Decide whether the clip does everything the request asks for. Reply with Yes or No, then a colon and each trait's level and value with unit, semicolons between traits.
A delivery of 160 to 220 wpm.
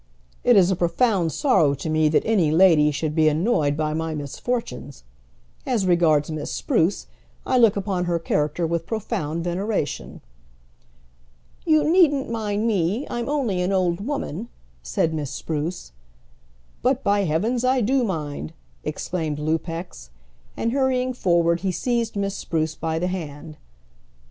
No: average, 145 wpm